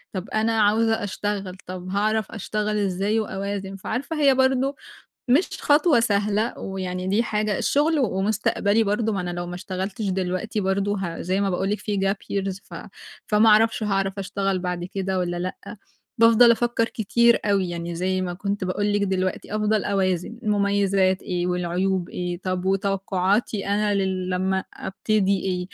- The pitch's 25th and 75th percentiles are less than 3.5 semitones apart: Yes, narrow, 2.4 semitones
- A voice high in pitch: Yes, high, 195 Hz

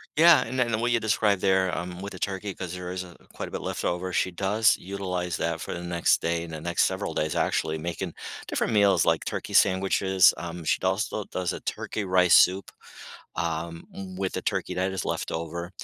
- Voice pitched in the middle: No, very low, 90 Hz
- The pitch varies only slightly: Yes, narrow, 2.2 semitones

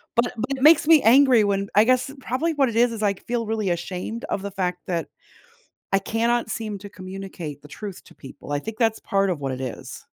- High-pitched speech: Yes, high, 215 Hz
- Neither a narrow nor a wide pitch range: Yes, average, 4.3 semitones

